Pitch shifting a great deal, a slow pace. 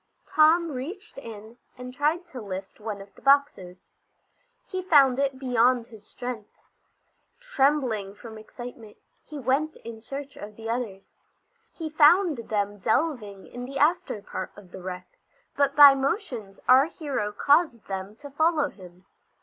No: wide, 5.8 semitones; average, 150 wpm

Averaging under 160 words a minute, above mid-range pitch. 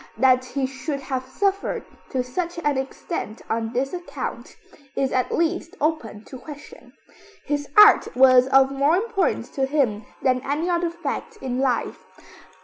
Yes: average, 150 wpm; very high, 275 Hz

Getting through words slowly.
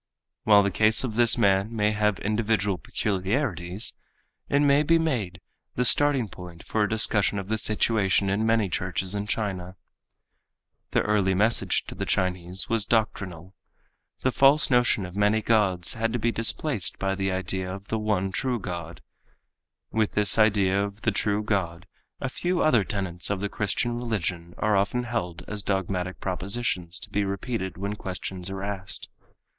No: average, 165 wpm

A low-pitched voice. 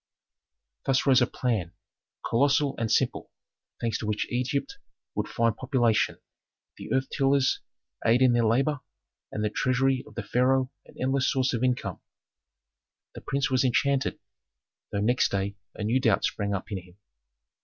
Yes: low, 125 Hz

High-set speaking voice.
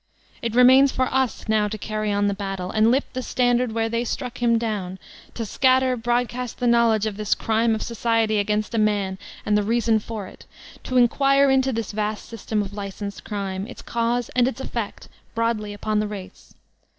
Yes: high, 225 Hz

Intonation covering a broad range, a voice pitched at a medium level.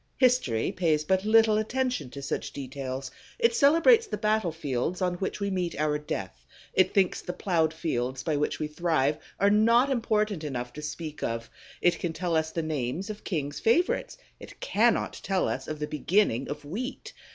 Yes: wide, 6.4 semitones; medium, 170 Hz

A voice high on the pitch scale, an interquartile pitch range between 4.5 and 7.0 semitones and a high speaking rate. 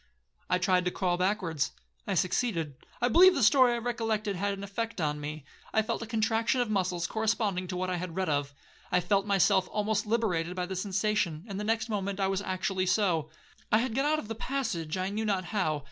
No: high, 195 Hz; average, 3.6 semitones; fast, 210 wpm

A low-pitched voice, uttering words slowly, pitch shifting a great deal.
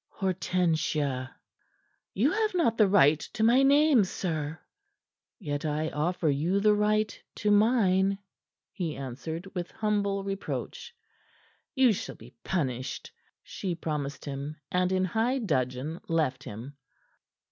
No: medium, 180 Hz; slow, 125 wpm; wide, 6.1 semitones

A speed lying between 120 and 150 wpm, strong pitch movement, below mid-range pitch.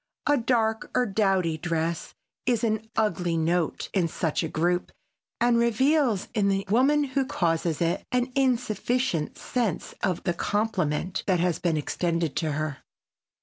No: average, 145 wpm; wide, 6.0 semitones; high, 195 Hz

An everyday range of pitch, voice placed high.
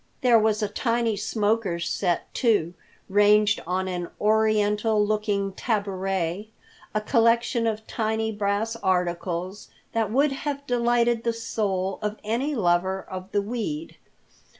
Yes: average, 3.0 semitones; high, 210 Hz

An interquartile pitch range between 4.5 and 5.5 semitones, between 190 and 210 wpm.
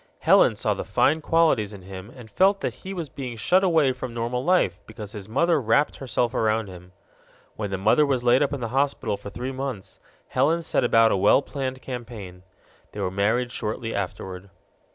Yes: average, 5.2 semitones; average, 195 wpm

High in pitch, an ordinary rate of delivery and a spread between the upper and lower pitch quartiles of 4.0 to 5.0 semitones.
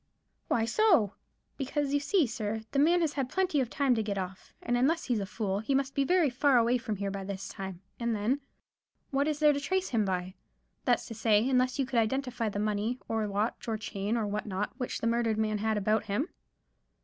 No: high, 230 Hz; fast, 220 wpm; average, 4.7 semitones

